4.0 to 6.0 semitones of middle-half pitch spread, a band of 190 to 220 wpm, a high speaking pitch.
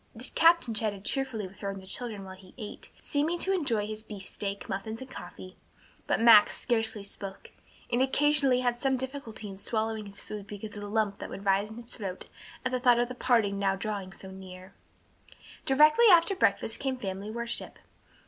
Yes: average, 4.3 semitones; average, 195 wpm; high, 220 Hz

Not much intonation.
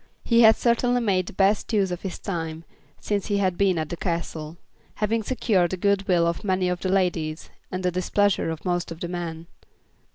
No: average, 3.0 semitones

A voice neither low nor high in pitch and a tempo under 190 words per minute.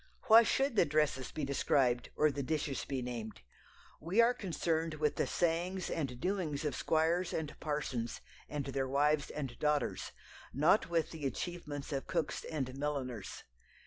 Yes: medium, 150 Hz; average, 155 wpm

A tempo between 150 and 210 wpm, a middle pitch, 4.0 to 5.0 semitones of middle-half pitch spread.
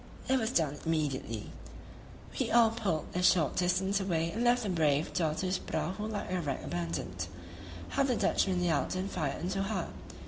Yes: average, 170 wpm; medium, 180 Hz; average, 4.6 semitones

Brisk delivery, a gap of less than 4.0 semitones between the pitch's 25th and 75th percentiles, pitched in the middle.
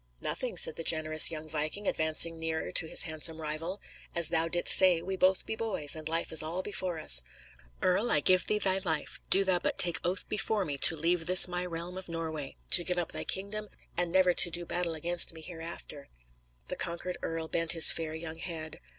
Yes: fast, 210 wpm; narrow, 2.4 semitones; medium, 170 Hz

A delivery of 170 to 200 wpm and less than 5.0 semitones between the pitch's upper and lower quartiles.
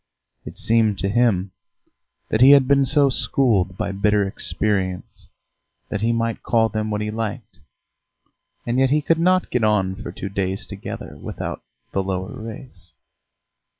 No: average, 155 wpm; average, 4.0 semitones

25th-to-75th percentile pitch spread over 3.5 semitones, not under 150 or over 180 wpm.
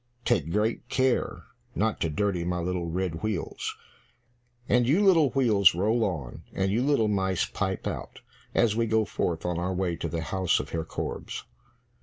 Yes: average, 4.6 semitones; average, 175 wpm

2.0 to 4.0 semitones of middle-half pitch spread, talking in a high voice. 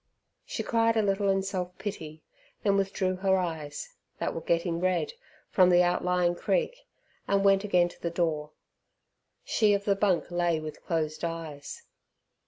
No: average, 2.8 semitones; medium, 180 Hz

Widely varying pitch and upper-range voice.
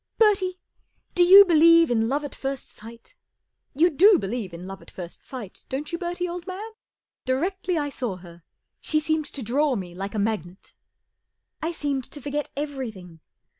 Yes: wide, 7.9 semitones; very high, 285 Hz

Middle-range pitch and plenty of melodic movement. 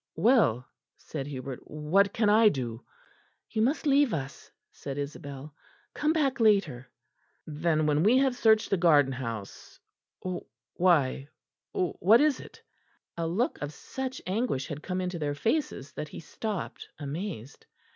Yes: medium, 170 Hz; wide, 7.6 semitones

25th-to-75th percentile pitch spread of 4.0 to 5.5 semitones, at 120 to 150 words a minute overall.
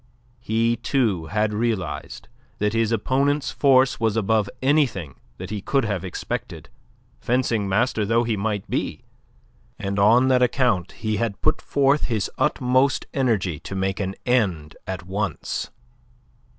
Yes: average, 4.3 semitones; average, 140 wpm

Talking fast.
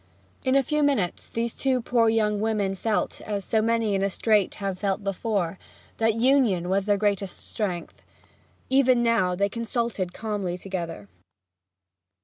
No: average, 155 wpm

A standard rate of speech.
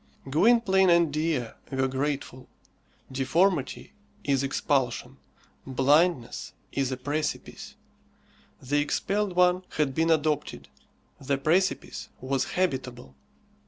No: slow, 95 wpm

